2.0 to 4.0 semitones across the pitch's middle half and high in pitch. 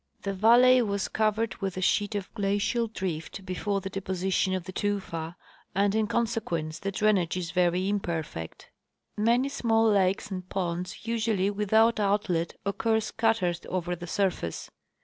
Yes: average, 3.1 semitones; high, 195 Hz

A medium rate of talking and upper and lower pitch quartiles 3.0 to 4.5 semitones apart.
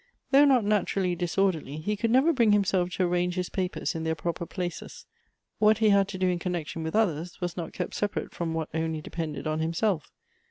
No: fast, 210 wpm; average, 4.0 semitones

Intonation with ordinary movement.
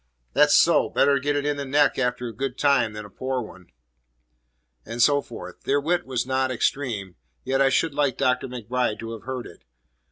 Yes: average, 3.2 semitones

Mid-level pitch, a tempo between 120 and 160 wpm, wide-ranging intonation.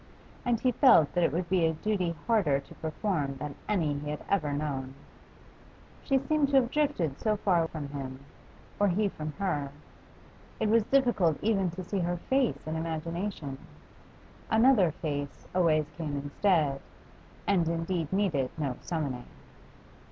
Yes: medium, 170 Hz; average, 150 wpm; wide, 5.7 semitones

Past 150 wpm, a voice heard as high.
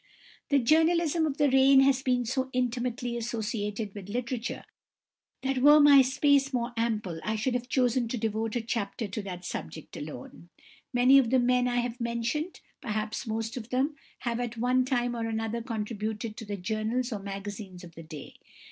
Yes: average, 180 wpm; high, 235 Hz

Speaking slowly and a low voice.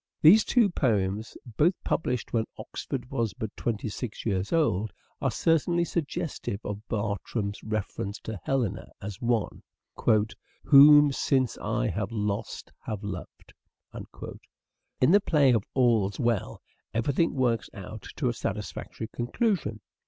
Yes: slow, 130 wpm; low, 115 Hz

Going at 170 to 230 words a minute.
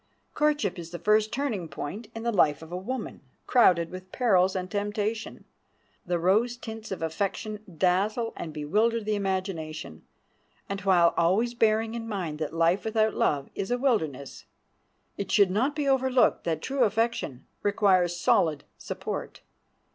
No: average, 155 wpm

